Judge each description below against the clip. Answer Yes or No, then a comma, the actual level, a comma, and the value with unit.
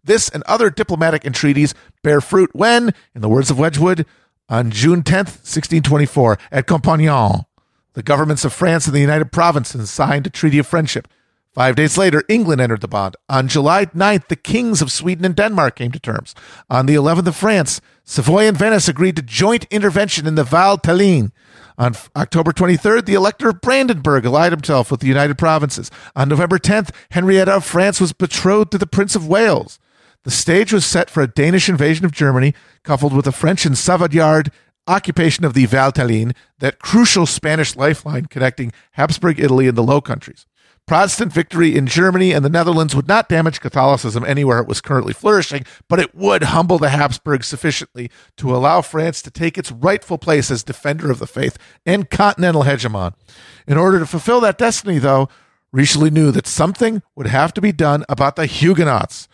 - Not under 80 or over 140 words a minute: No, average, 185 wpm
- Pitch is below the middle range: No, medium, 155 Hz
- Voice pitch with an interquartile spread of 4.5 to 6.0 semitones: Yes, average, 5.0 semitones